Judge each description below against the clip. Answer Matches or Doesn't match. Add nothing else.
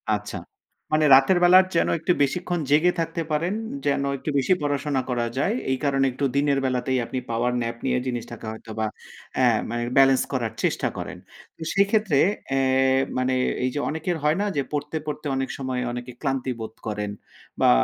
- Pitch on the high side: Doesn't match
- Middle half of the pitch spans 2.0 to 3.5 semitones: Doesn't match